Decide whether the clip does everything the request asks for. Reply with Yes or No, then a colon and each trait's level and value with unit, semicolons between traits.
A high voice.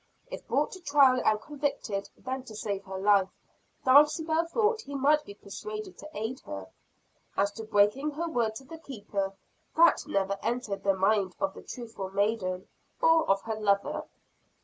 Yes: high, 225 Hz